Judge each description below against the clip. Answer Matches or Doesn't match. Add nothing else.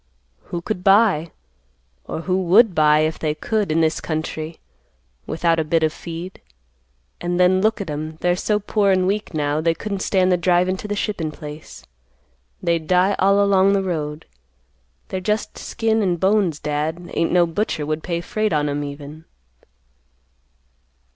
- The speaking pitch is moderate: Matches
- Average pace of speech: Matches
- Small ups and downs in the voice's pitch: Doesn't match